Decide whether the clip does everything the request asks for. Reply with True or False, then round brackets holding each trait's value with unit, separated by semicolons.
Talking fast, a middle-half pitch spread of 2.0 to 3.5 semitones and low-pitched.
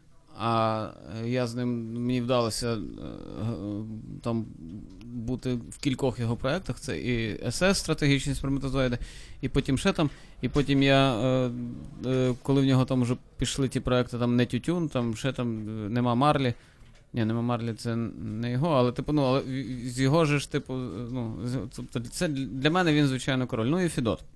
True (160 wpm; 2.5 semitones; 125 Hz)